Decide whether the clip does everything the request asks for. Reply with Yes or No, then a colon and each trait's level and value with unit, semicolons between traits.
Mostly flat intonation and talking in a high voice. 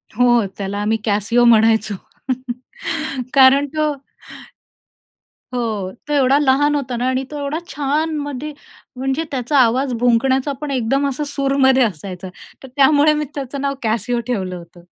No: average, 3.6 semitones; very high, 260 Hz